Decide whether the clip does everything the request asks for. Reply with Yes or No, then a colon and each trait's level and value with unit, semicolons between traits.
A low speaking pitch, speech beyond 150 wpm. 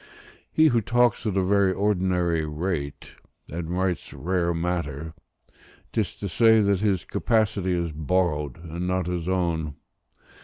No: very low, 90 Hz; average, 140 wpm